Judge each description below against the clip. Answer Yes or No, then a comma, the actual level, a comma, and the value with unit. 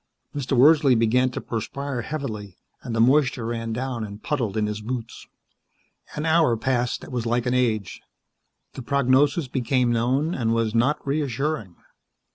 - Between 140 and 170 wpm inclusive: Yes, average, 155 wpm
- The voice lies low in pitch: Yes, low, 125 Hz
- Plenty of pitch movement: No, average, 3.4 semitones